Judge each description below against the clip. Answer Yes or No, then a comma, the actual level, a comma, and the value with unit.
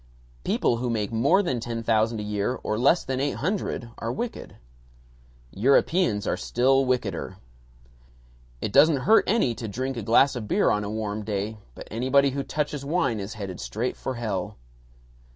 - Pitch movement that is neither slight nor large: Yes, average, 4.1 semitones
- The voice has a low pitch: Yes, low, 120 Hz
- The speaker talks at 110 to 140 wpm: No, average, 170 wpm